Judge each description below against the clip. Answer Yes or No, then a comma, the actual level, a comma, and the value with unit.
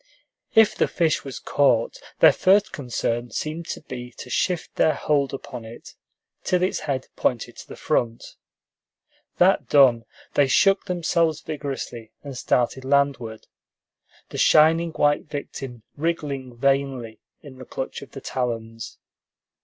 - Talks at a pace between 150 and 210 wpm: No, average, 140 wpm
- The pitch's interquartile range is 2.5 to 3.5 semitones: No, average, 4.3 semitones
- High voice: No, medium, 140 Hz